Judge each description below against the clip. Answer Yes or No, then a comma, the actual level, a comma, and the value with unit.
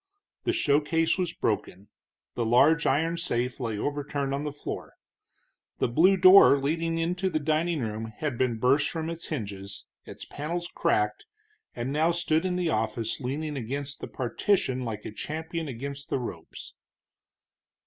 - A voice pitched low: No, medium, 145 Hz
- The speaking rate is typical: Yes, average, 155 wpm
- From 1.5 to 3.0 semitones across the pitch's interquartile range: No, average, 5.3 semitones